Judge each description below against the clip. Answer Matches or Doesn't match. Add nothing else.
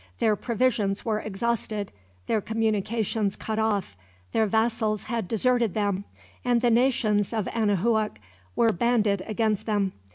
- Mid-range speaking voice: Doesn't match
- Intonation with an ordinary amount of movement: Doesn't match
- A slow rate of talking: Matches